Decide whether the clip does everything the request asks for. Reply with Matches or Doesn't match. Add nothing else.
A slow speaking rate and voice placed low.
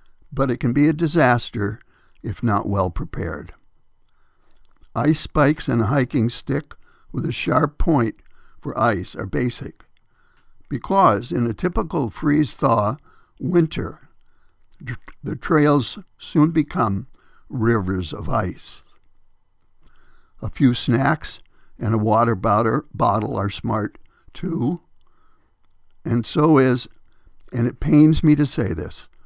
Matches